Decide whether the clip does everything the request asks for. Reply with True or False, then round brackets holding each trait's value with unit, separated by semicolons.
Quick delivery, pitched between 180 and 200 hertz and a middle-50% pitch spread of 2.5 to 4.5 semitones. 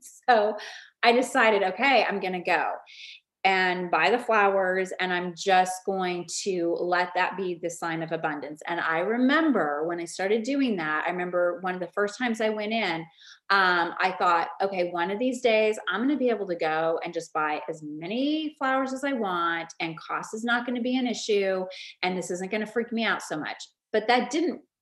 False (215 wpm; 190 Hz; 5.3 semitones)